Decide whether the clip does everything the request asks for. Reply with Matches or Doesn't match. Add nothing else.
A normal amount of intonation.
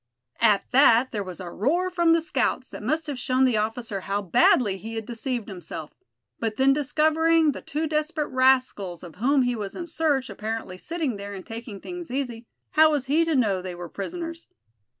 Doesn't match